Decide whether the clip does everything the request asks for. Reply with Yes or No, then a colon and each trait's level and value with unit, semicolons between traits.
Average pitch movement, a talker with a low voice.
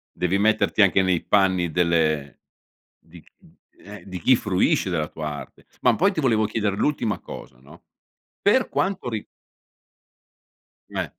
Yes: average, 4.5 semitones; very low, 95 Hz